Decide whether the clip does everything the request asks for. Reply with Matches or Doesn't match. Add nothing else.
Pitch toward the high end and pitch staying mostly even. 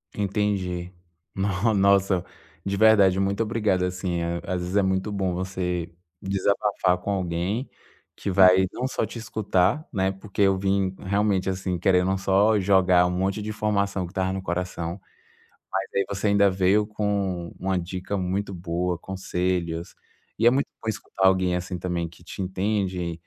Doesn't match